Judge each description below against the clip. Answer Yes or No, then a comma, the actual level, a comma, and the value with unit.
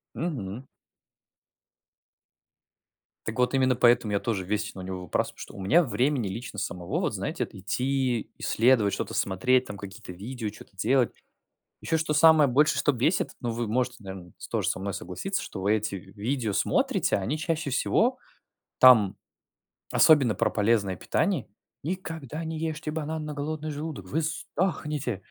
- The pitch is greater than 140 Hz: No, low, 125 Hz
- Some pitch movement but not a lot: No, wide, 7.0 semitones